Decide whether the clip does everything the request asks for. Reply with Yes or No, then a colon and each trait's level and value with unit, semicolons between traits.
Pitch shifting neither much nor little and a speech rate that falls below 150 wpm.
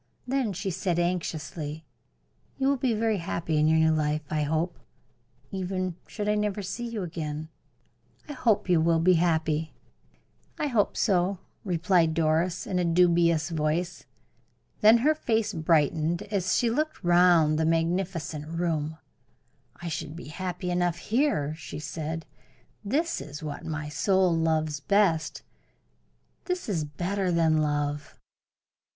Yes: average, 3.6 semitones; average, 140 wpm